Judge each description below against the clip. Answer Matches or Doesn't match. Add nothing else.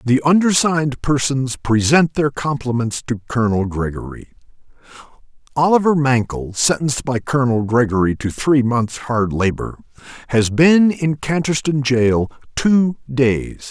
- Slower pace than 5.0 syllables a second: Matches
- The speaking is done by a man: Matches